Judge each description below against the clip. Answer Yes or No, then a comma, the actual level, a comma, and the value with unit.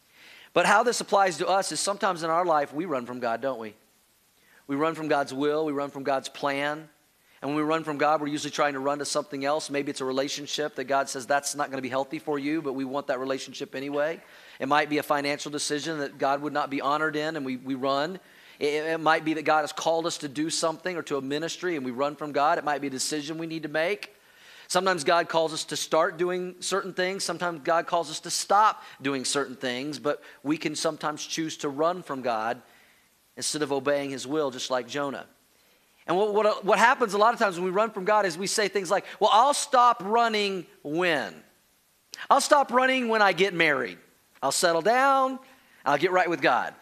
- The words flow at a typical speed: No, fast, 235 wpm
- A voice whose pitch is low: No, medium, 155 Hz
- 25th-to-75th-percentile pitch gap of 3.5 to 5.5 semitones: Yes, average, 4.2 semitones